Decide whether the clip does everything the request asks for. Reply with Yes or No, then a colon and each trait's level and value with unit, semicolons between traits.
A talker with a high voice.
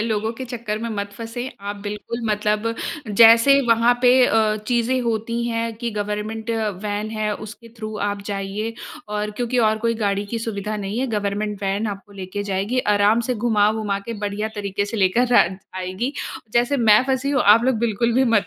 Yes: high, 215 Hz